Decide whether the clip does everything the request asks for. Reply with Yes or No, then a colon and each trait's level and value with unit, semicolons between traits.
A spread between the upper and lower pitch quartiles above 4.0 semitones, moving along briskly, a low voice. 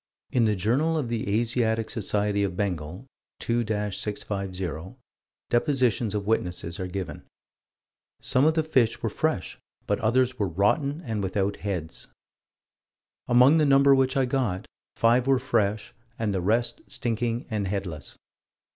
No: average, 4.4 semitones; average, 140 wpm; low, 110 Hz